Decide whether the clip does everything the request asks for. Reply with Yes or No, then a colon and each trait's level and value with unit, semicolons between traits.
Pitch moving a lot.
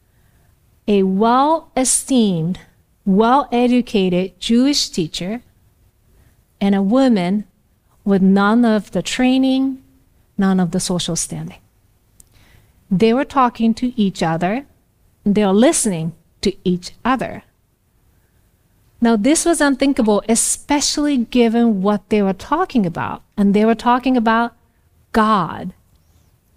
Yes: wide, 5.8 semitones